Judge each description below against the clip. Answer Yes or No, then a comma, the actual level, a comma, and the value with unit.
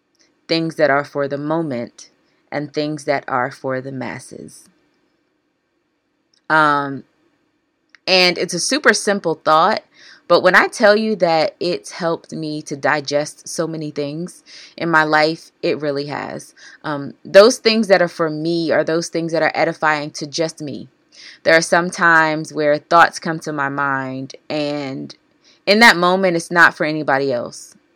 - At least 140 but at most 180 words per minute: Yes, average, 160 wpm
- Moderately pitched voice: Yes, medium, 165 Hz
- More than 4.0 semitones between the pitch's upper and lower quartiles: Yes, average, 5.0 semitones